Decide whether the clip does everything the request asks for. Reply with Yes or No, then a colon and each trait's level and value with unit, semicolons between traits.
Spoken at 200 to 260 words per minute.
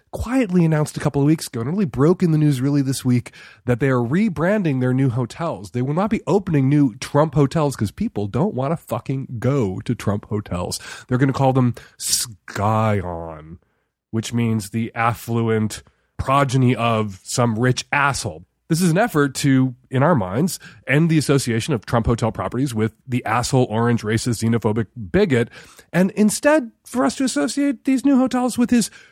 No: average, 185 wpm